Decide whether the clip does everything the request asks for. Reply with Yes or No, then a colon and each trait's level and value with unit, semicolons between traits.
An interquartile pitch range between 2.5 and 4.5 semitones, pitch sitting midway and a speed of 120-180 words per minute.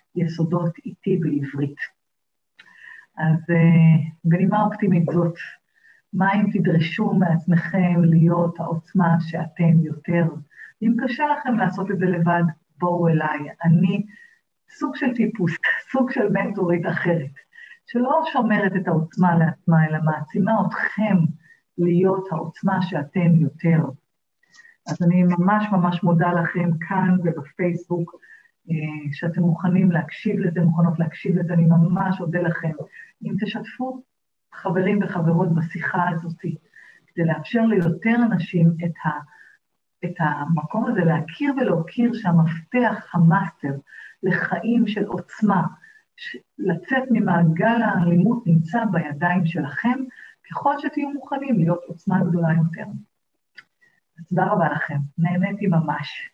No: average, 3.8 semitones; medium, 175 Hz; average, 110 wpm